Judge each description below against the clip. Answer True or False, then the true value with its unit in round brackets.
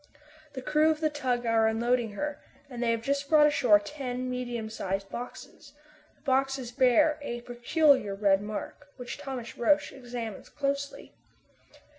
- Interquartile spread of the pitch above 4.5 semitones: False (3.5 semitones)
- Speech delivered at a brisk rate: False (150 wpm)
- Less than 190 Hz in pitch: False (250 Hz)